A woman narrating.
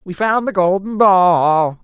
No: male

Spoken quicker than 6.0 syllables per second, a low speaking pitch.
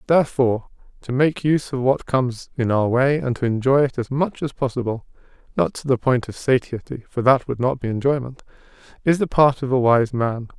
No: 4.1 syllables/s; low, 130 Hz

